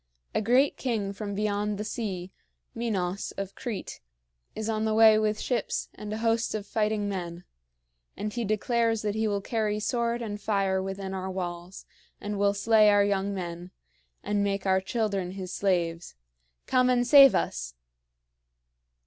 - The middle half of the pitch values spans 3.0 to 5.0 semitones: No, narrow, 2.4 semitones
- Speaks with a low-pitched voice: No, high, 205 Hz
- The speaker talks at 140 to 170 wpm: Yes, average, 160 wpm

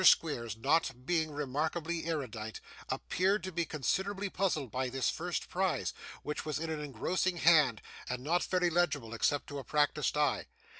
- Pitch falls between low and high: Yes, medium, 155 Hz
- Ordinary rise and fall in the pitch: Yes, average, 4.5 semitones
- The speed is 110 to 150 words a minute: No, average, 160 wpm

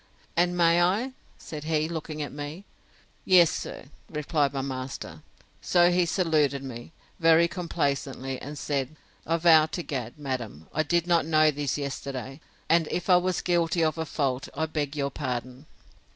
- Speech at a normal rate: Yes, average, 165 wpm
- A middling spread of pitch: Yes, average, 3.5 semitones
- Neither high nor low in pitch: Yes, medium, 155 Hz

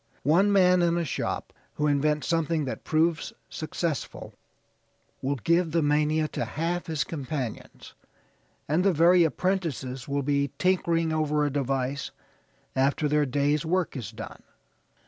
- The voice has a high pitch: No, medium, 155 Hz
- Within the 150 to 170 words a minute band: No, average, 140 wpm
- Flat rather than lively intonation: No, average, 3.1 semitones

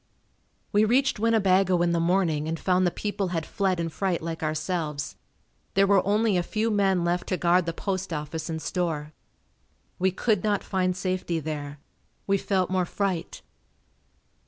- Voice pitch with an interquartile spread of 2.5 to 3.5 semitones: Yes, average, 3.0 semitones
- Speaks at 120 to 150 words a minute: No, average, 165 wpm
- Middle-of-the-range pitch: Yes, medium, 180 Hz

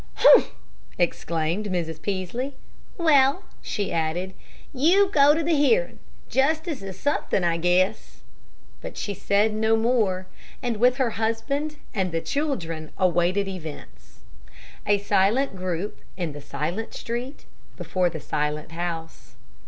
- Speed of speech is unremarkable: No, slow, 130 wpm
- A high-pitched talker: Yes, high, 200 Hz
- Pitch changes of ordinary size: No, wide, 7.3 semitones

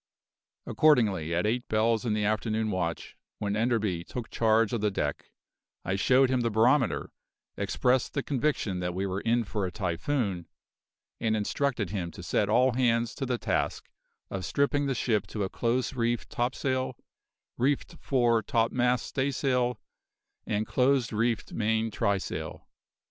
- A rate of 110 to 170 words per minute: Yes, average, 150 wpm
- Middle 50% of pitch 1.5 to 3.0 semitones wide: No, average, 3.5 semitones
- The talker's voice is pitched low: Yes, low, 115 Hz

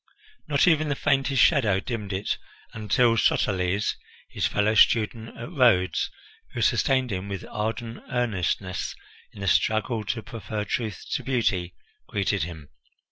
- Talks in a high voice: No, low, 110 Hz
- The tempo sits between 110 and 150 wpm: Yes, slow, 135 wpm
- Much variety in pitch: No, average, 3.9 semitones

